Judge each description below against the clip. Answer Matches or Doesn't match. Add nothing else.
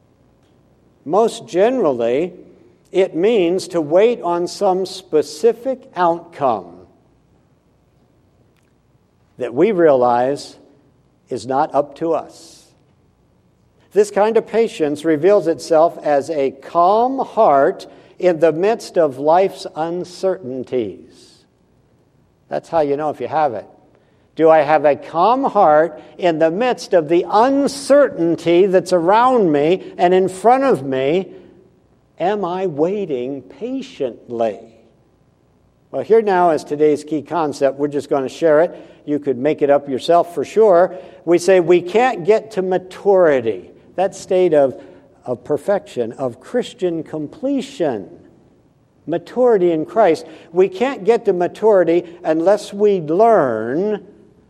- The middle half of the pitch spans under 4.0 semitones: Doesn't match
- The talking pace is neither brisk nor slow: Doesn't match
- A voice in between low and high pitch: Matches